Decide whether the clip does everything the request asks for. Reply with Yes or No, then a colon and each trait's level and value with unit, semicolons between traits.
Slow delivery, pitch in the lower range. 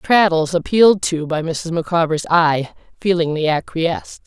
No: slow, 125 wpm; medium, 170 Hz